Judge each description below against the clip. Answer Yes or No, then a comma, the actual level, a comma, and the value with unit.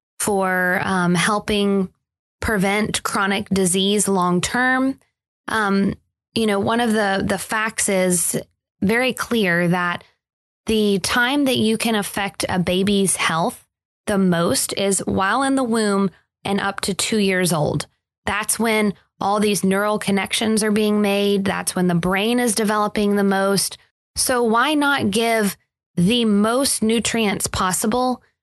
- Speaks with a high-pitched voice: Yes, high, 205 Hz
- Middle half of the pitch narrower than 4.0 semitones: Yes, narrow, 2.5 semitones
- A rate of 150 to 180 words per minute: No, average, 140 wpm